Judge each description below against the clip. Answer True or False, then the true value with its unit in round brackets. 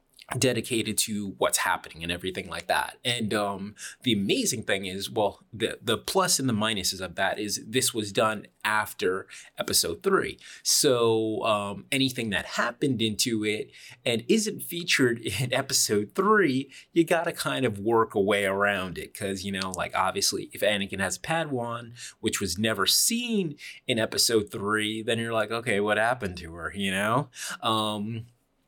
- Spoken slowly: False (165 wpm)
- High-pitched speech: False (110 Hz)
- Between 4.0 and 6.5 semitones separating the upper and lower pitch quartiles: True (4.3 semitones)